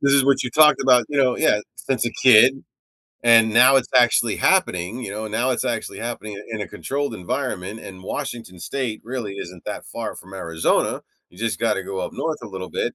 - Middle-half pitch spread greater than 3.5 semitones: Yes, average, 4.7 semitones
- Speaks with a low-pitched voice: Yes, low, 115 Hz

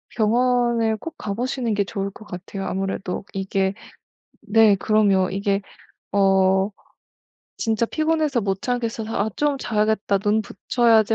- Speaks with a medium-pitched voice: No, high, 215 Hz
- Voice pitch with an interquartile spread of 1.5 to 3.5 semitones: Yes, average, 3.1 semitones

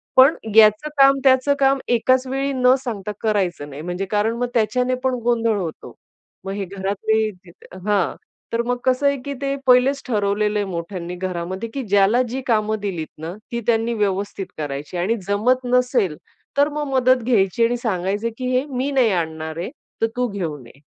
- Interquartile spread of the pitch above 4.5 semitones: Yes, average, 5.0 semitones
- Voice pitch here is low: No, high, 220 Hz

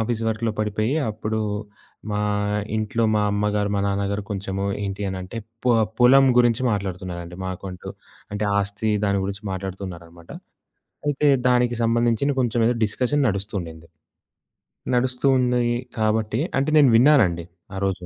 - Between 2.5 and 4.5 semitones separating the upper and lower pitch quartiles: Yes, average, 3.7 semitones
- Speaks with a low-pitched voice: Yes, low, 105 Hz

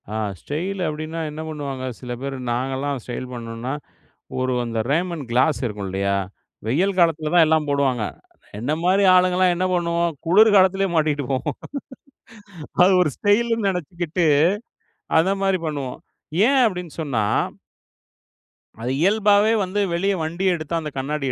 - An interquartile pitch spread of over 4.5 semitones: Yes, wide, 5.4 semitones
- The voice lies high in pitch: No, medium, 160 Hz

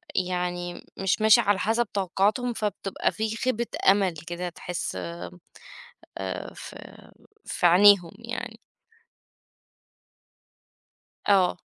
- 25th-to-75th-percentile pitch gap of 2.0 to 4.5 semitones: Yes, average, 3.5 semitones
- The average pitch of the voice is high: Yes, high, 195 Hz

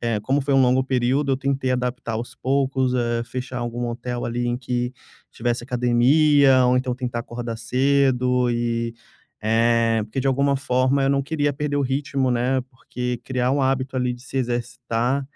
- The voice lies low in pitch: Yes, low, 125 Hz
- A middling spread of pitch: No, narrow, 2.0 semitones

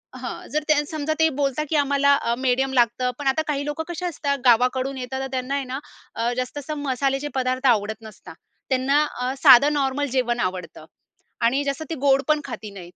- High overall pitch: Yes, very high, 270 Hz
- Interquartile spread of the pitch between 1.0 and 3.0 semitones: Yes, narrow, 2.5 semitones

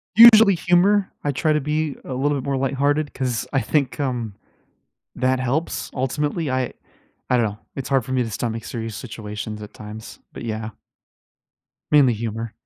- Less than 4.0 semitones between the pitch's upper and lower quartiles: No, average, 4.4 semitones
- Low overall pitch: Yes, low, 130 Hz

